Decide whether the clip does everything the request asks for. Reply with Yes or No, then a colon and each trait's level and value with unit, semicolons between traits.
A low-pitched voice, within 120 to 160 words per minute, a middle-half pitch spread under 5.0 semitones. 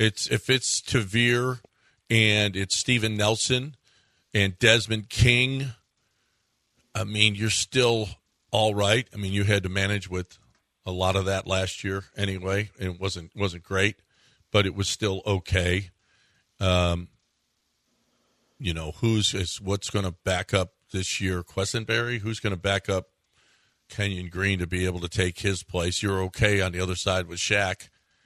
Yes: low, 100 Hz; average, 155 wpm; average, 3.0 semitones